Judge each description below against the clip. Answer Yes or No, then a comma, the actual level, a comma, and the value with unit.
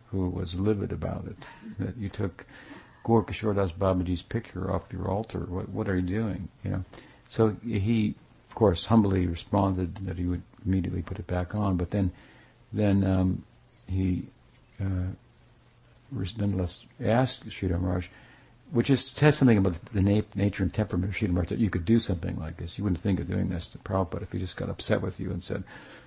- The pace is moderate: Yes, average, 190 wpm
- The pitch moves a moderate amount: Yes, average, 3.4 semitones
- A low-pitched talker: Yes, very low, 95 Hz